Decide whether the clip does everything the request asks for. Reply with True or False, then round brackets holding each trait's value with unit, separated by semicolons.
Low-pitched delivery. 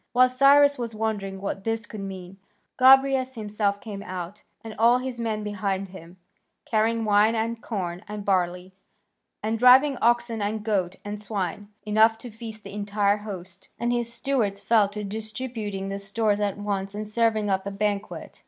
False (210 Hz)